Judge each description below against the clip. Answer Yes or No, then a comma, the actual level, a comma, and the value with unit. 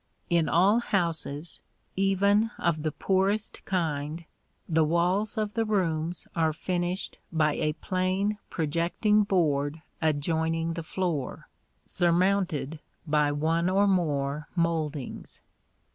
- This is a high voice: No, medium, 170 Hz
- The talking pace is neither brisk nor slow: No, slow, 110 wpm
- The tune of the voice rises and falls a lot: No, average, 3.5 semitones